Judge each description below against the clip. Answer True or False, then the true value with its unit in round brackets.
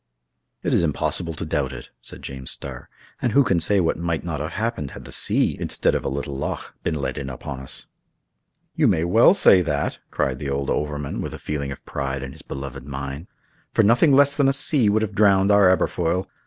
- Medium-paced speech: False (220 wpm)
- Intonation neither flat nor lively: False (6.6 semitones)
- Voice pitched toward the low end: True (80 Hz)